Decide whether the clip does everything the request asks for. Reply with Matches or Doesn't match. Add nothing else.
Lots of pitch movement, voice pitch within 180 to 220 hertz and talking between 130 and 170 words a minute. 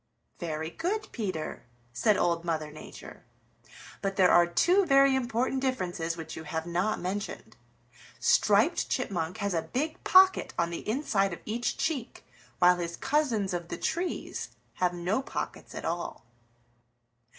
Matches